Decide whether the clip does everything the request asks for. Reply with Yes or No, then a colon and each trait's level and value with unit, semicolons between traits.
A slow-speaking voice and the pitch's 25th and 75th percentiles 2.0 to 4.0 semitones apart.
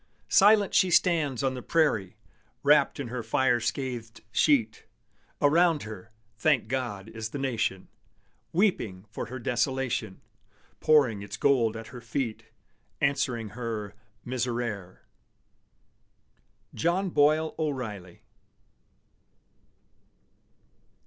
No: slow, 100 wpm; average, 4.7 semitones